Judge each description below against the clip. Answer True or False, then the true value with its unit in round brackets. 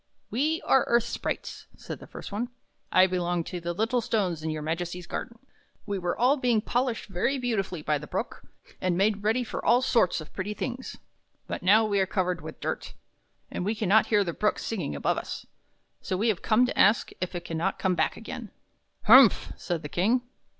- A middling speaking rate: False (215 wpm)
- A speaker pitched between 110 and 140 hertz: False (200 Hz)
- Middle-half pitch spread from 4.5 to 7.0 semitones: True (4.8 semitones)